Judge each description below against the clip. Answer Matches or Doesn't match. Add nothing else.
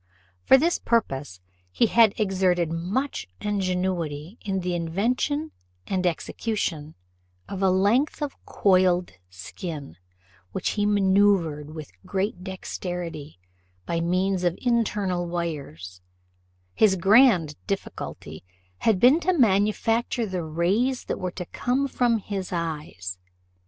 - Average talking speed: Doesn't match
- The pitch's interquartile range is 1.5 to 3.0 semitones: Doesn't match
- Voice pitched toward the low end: Doesn't match